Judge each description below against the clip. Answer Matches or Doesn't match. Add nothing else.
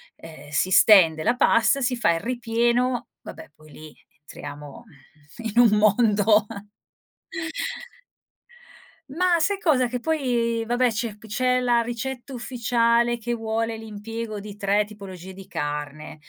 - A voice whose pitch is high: Matches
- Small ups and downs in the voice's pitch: Doesn't match